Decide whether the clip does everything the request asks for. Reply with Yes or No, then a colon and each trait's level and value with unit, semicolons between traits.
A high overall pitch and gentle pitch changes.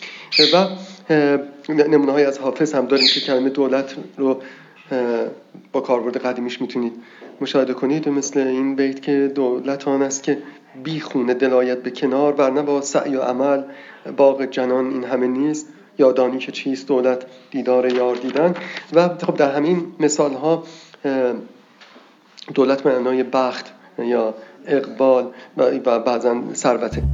No: low, 135 Hz; narrow, 2.2 semitones